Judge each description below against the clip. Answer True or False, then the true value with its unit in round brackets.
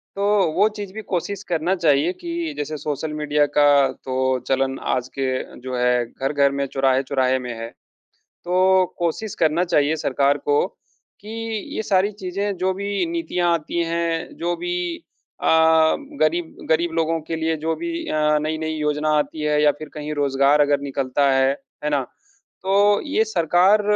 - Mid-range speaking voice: True (155 Hz)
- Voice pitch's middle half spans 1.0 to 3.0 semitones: False (4.3 semitones)